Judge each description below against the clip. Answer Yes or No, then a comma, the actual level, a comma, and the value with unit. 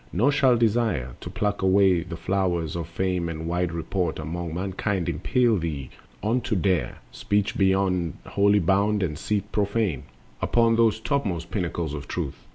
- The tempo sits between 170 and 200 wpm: No, average, 155 wpm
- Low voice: Yes, very low, 95 Hz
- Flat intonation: No, average, 3.7 semitones